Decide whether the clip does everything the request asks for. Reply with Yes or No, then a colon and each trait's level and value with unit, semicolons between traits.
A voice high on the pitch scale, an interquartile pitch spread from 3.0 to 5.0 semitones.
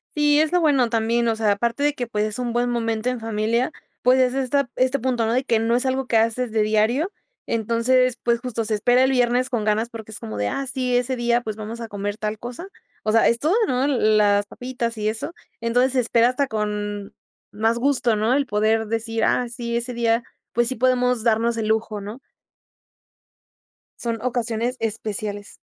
No: high, 235 Hz; narrow, 2.4 semitones